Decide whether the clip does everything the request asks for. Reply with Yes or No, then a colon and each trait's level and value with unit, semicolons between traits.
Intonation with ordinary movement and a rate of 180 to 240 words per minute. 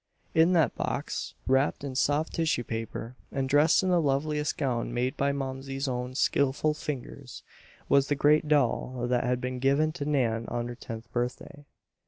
No: average, 3.1 semitones; average, 170 wpm